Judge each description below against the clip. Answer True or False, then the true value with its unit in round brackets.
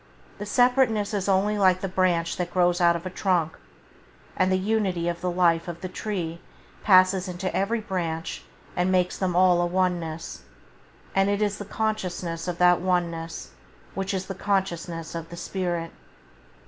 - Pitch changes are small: True (2.1 semitones)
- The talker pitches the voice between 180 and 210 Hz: True (185 Hz)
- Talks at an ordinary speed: True (175 wpm)